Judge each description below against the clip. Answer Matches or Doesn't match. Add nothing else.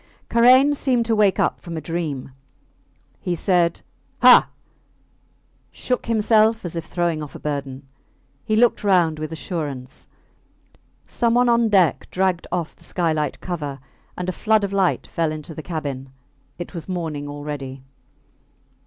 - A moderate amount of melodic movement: Doesn't match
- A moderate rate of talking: Matches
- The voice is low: Doesn't match